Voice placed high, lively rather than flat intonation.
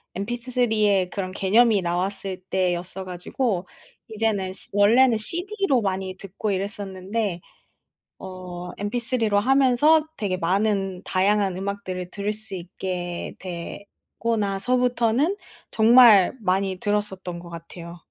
No: high, 200 Hz; average, 3.4 semitones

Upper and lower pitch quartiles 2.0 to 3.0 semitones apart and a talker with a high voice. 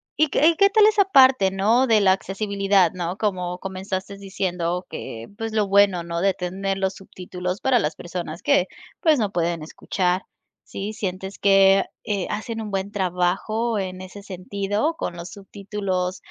Yes: narrow, 2.4 semitones; high, 195 Hz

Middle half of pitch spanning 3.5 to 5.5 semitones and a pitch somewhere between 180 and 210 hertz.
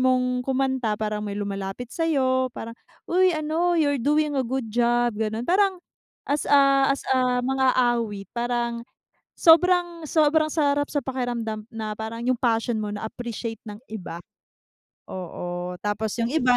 No: average, 4.5 semitones; high, 245 Hz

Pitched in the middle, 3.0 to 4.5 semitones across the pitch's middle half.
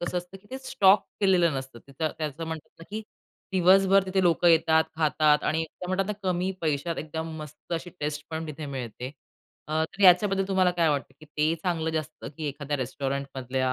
Yes: medium, 160 Hz; average, 3.5 semitones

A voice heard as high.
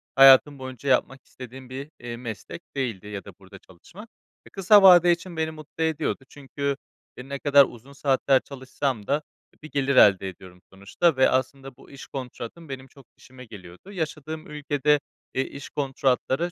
No: low, 135 Hz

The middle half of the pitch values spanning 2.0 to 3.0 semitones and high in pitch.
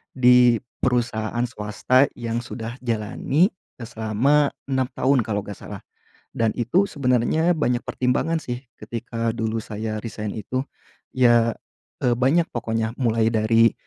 No: narrow, 2.4 semitones; low, 120 Hz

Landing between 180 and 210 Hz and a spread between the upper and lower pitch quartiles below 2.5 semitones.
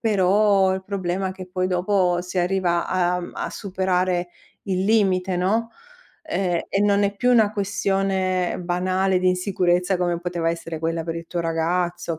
Yes: medium, 185 Hz; narrow, 1.8 semitones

